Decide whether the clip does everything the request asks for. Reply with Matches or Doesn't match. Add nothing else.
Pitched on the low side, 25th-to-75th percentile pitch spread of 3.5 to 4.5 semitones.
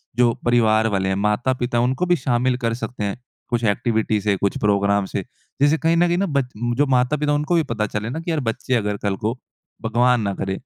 Matches